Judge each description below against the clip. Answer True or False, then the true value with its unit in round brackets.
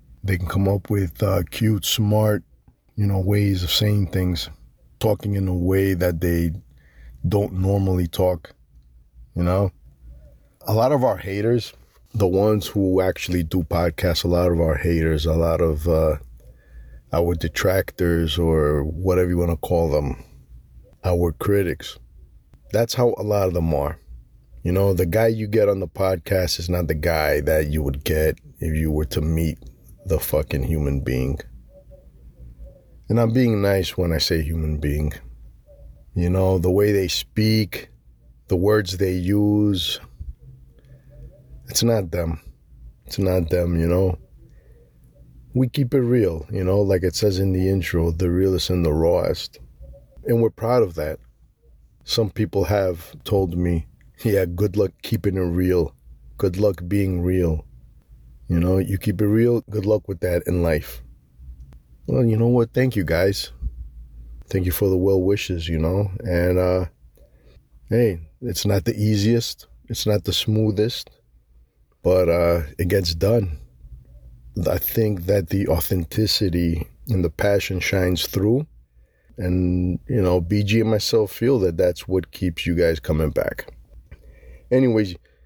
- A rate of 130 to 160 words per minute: True (155 wpm)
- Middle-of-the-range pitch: False (90 Hz)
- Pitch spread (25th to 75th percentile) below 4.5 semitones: False (5.2 semitones)